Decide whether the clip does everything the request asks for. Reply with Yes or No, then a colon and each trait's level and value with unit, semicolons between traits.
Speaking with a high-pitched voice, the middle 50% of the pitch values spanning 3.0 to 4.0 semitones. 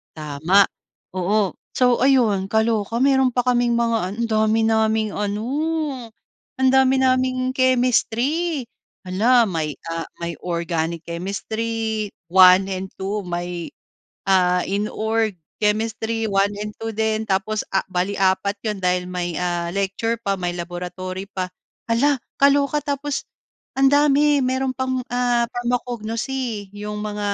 No: high, 215 Hz; average, 4.7 semitones